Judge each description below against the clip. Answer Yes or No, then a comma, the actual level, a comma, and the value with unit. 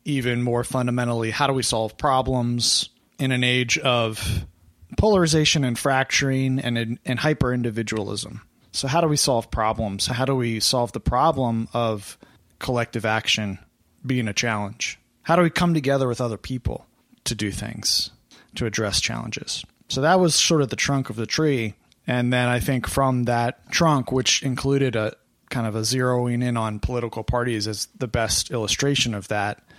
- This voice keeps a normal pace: Yes, average, 170 wpm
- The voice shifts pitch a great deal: No, average, 3.1 semitones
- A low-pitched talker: Yes, low, 120 Hz